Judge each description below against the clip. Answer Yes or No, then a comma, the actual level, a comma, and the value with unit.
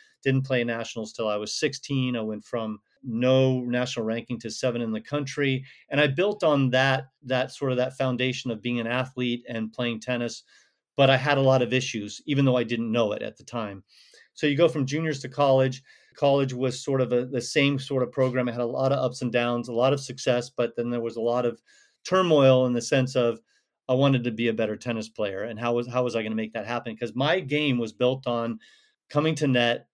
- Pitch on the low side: Yes, low, 125 Hz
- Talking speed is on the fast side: Yes, fast, 240 wpm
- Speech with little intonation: Yes, narrow, 2.2 semitones